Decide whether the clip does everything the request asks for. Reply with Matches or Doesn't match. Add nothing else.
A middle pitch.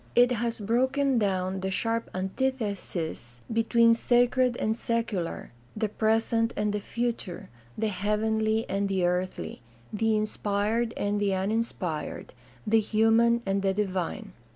Doesn't match